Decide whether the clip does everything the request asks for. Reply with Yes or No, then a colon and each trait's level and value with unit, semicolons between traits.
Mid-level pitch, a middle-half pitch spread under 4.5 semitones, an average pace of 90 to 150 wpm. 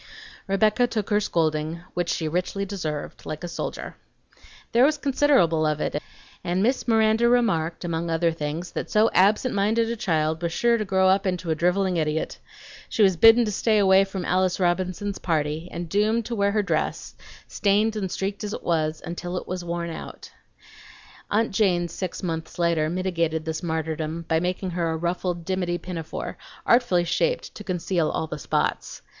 No: medium, 180 Hz; average, 4.0 semitones; average, 180 wpm